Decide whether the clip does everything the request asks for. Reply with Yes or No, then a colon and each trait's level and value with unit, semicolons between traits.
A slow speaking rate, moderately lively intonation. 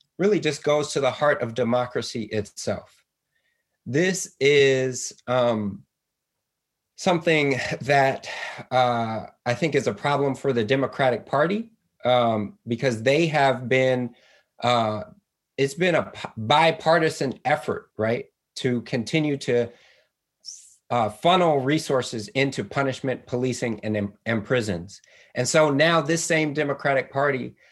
Yes: slow, 120 wpm; average, 3.8 semitones